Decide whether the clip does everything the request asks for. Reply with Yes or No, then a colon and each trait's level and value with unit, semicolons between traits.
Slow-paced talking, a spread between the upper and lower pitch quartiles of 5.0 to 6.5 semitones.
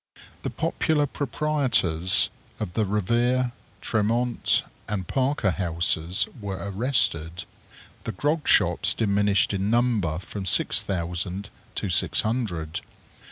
Yes: slow, 110 wpm; average, 5.3 semitones